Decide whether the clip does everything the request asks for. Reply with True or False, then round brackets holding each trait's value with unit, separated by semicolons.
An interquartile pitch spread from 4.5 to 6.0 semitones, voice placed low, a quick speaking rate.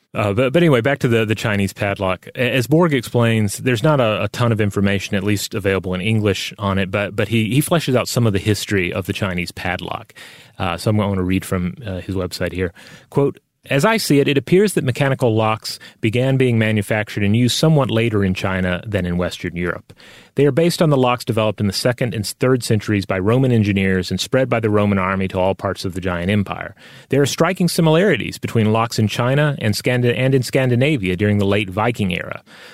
True (4.9 semitones; 110 Hz; 225 wpm)